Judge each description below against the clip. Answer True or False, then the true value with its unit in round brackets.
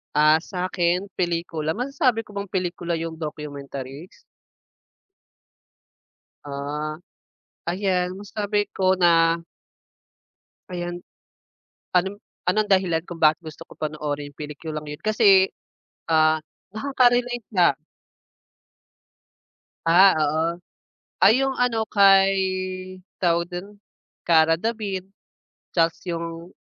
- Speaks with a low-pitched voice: False (175 Hz)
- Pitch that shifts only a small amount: False (3.9 semitones)